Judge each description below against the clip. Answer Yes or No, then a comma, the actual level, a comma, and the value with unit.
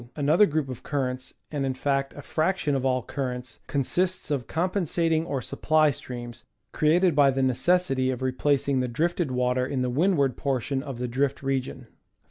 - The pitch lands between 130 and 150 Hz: Yes, low, 135 Hz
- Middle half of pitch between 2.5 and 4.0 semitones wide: Yes, average, 3.5 semitones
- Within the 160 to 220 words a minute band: Yes, average, 175 wpm